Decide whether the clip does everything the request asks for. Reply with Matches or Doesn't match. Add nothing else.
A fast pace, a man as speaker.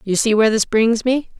Doesn't match